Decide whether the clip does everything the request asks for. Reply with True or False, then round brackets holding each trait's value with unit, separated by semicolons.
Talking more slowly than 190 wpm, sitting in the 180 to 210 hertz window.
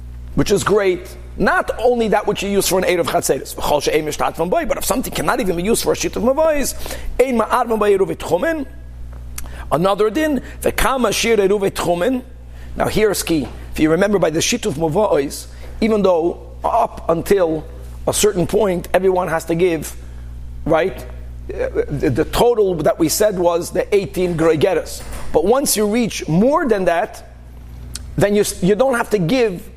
True (150 wpm; 190 Hz)